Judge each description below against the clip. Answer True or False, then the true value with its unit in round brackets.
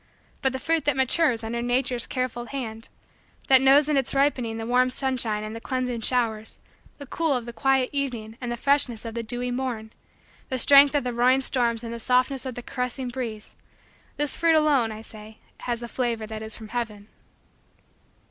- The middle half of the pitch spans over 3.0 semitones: False (2.7 semitones)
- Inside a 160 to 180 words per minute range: False (195 wpm)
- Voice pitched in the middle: False (245 Hz)